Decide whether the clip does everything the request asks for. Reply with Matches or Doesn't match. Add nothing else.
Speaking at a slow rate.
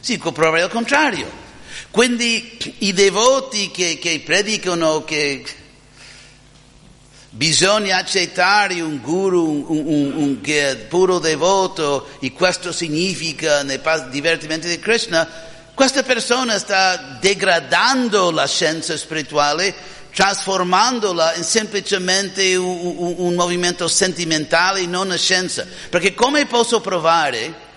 Matches